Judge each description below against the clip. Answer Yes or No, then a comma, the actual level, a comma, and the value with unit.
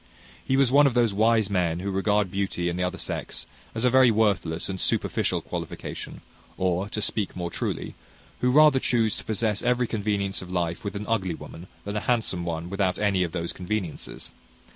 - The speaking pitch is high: No, low, 100 Hz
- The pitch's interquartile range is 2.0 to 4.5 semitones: Yes, average, 3.8 semitones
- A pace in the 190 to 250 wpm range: Yes, average, 195 wpm